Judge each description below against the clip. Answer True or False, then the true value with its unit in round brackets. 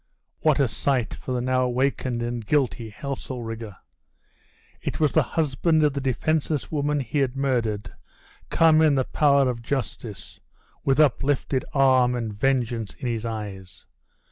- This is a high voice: False (130 Hz)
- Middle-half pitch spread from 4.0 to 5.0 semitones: False (3.2 semitones)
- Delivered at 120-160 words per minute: True (145 wpm)